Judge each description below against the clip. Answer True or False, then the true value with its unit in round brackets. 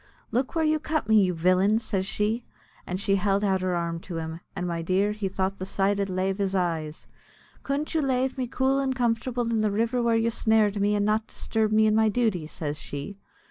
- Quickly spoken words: True (225 wpm)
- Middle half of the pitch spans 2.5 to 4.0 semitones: True (3.7 semitones)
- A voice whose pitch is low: False (210 Hz)